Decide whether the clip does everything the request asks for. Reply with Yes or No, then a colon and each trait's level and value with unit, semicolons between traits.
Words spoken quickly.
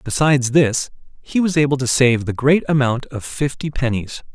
No: average, 180 wpm